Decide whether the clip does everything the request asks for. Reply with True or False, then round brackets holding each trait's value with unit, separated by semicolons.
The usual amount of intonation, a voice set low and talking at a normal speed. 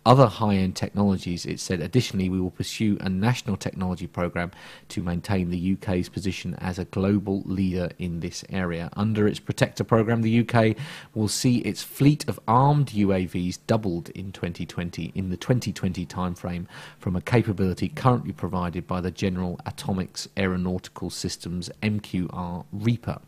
True (3.6 semitones; 95 Hz; 150 wpm)